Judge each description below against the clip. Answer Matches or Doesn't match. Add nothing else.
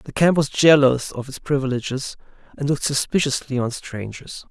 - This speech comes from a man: Matches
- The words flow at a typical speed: Matches